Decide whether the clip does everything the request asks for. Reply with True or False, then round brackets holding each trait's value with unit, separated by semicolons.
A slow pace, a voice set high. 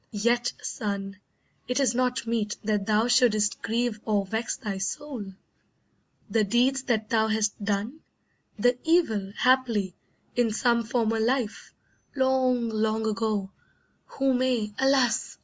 True (130 wpm; 225 Hz)